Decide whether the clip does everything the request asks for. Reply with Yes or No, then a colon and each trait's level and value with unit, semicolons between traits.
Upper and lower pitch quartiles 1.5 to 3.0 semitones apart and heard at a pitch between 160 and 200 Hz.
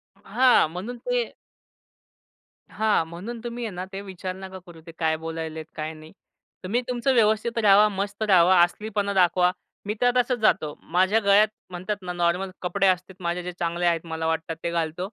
No: average, 3.8 semitones; medium, 185 Hz